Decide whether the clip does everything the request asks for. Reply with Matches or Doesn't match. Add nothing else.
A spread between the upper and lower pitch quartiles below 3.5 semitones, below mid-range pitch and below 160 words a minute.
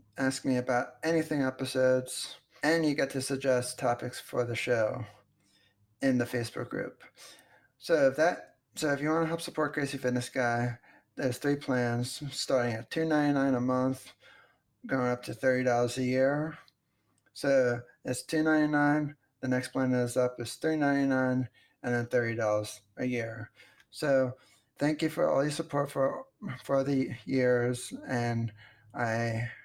Matches